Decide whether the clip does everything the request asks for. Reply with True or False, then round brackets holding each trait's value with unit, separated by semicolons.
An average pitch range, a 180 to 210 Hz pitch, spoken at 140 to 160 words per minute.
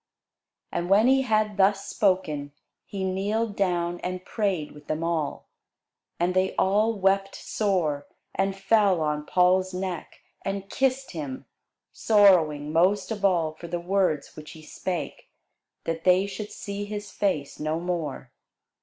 True (3.6 semitones; 185 Hz; 145 wpm)